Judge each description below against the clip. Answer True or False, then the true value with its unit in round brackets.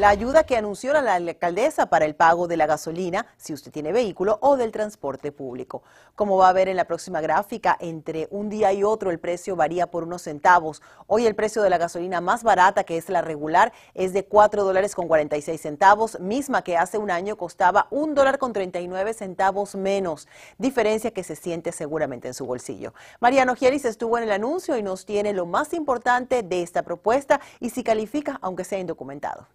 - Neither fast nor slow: False (205 wpm)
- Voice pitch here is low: False (190 Hz)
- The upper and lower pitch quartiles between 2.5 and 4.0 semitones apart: False (4.5 semitones)